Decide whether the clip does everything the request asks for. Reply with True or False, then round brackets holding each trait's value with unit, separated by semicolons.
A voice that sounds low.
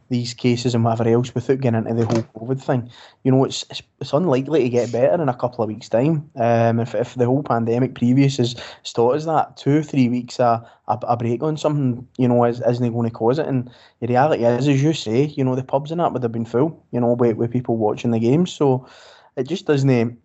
True (125 Hz)